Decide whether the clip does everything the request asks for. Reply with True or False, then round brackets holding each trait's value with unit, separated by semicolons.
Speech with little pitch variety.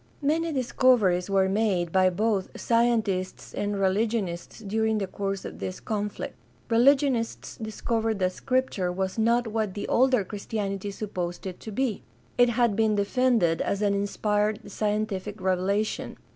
False (3.0 semitones)